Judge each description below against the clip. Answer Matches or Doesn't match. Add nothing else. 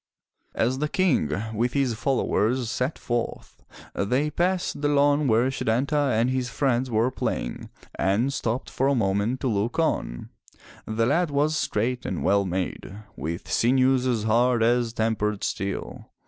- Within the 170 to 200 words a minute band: Doesn't match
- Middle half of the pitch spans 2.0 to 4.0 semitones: Matches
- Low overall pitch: Matches